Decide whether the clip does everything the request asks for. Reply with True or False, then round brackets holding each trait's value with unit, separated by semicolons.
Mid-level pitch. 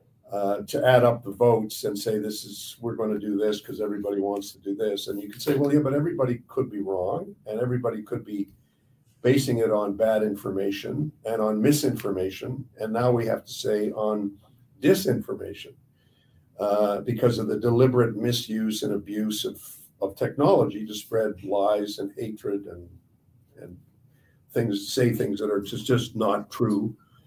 False (110 Hz)